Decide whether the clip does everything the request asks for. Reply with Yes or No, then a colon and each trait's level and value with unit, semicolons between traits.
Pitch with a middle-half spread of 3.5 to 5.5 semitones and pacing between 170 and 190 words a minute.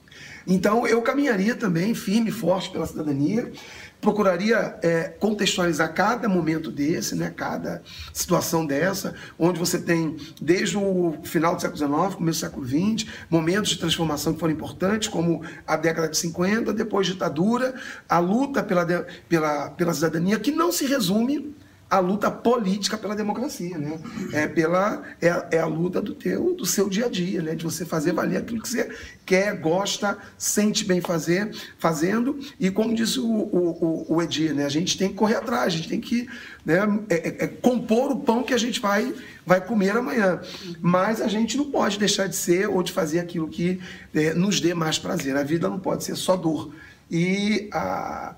Yes: average, 4.3 semitones; average, 180 wpm